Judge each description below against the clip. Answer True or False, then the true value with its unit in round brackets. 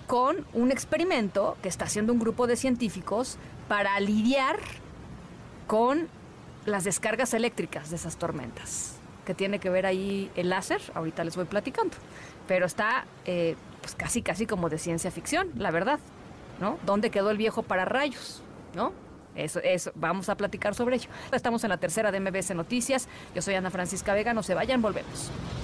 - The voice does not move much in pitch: False (4.6 semitones)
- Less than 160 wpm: False (170 wpm)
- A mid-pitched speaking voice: False (200 Hz)